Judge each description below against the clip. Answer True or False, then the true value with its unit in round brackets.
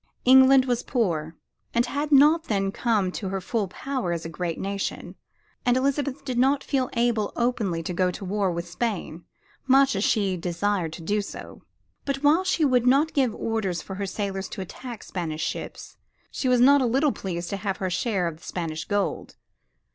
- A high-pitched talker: True (210 Hz)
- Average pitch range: False (6.0 semitones)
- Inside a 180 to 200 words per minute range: True (195 wpm)